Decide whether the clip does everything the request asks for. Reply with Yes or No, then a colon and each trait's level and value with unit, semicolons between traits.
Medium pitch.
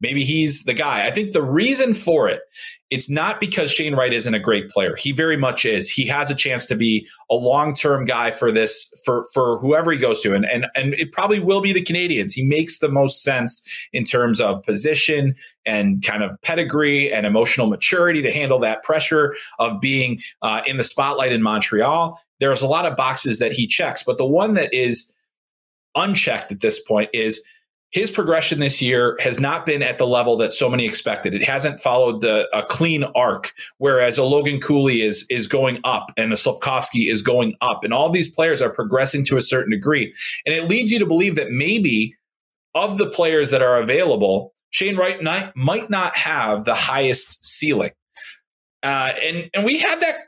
Yes: medium, 145 Hz